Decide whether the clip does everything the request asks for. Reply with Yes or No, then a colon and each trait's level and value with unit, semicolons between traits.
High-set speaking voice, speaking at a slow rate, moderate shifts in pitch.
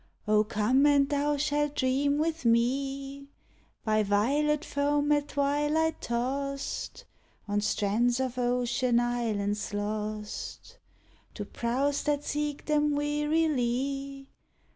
Yes: very high, 275 Hz; slow, 105 wpm; average, 3.7 semitones